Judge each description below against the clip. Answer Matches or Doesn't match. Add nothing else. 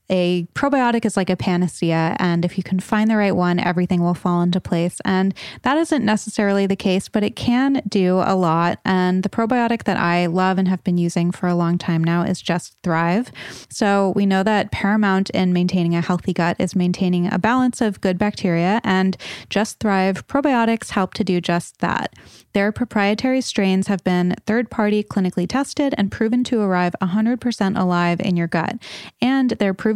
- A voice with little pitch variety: Doesn't match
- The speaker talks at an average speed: Matches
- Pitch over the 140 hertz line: Matches